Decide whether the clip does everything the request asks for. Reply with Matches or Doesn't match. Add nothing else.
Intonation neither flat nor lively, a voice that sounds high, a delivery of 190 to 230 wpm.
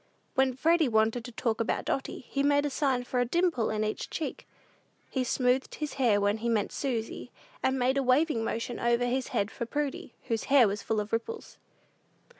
Matches